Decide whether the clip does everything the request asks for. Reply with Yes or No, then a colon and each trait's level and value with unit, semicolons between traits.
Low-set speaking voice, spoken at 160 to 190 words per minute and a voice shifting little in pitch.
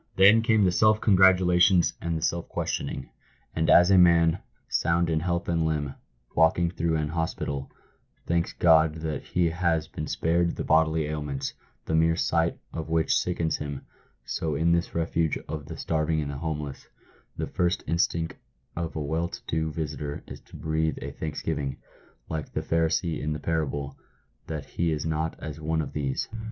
Yes: very low, 80 Hz; average, 175 wpm; narrow, 1.7 semitones